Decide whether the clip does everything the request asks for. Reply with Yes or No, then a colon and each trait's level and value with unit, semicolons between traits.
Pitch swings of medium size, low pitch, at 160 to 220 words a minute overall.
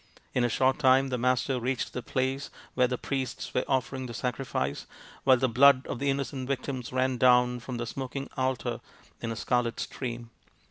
No: narrow, 1.4 semitones; low, 130 Hz; average, 185 wpm